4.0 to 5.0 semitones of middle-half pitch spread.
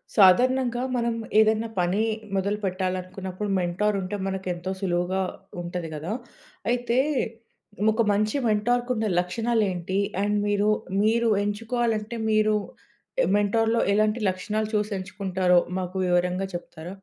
No: average, 3.2 semitones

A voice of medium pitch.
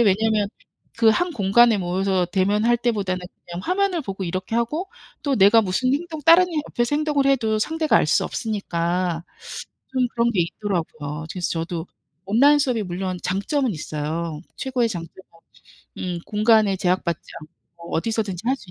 No: high, 210 Hz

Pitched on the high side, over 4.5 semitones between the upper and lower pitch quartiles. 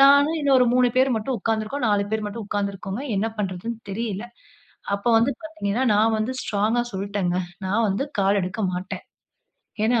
No: high, 220 Hz; average, 3.5 semitones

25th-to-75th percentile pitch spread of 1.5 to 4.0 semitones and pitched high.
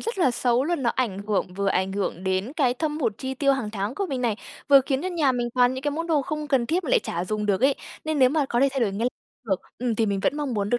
No: average, 5.3 semitones; very high, 250 Hz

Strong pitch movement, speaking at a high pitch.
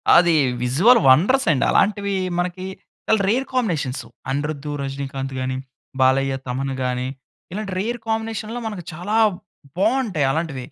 No: wide, 8.1 semitones; medium, 170 Hz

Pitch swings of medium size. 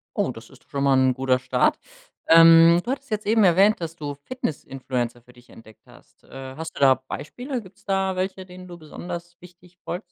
No: wide, 5.9 semitones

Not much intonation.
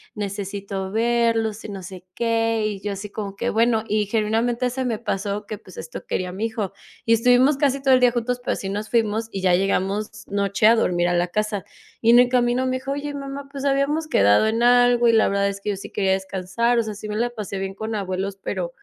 No: average, 3.4 semitones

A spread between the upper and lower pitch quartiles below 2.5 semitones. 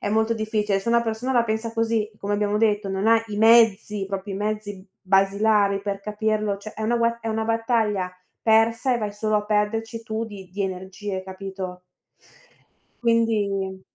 Yes: narrow, 2.1 semitones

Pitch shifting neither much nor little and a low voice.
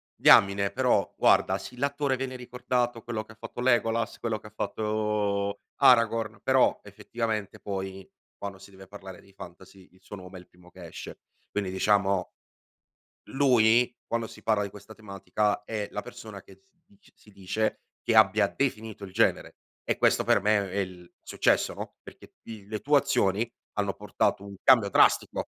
Yes: average, 3.0 semitones; low, 105 Hz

